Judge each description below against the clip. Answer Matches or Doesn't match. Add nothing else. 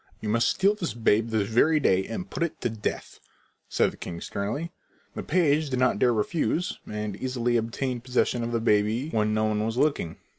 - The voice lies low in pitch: Matches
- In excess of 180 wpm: Matches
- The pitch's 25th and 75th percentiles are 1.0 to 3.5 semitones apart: Doesn't match